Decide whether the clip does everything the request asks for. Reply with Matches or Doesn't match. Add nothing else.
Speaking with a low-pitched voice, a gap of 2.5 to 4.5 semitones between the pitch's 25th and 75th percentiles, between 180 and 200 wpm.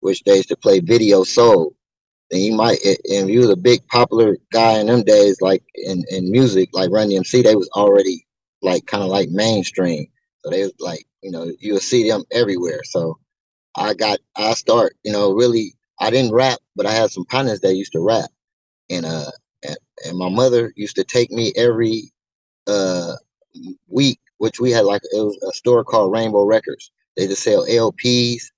Doesn't match